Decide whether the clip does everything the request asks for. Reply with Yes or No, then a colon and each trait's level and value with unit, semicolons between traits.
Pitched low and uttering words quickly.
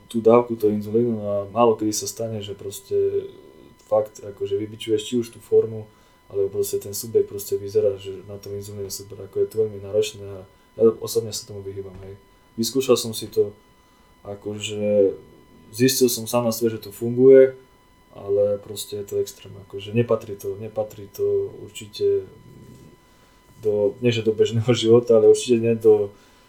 Yes: low, 115 Hz; fast, 170 wpm